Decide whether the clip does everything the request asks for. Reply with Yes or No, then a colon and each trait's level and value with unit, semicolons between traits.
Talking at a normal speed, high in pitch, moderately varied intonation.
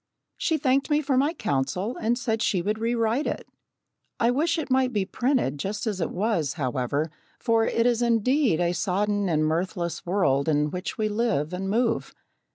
No: average, 180 wpm; high, 215 Hz; wide, 5.9 semitones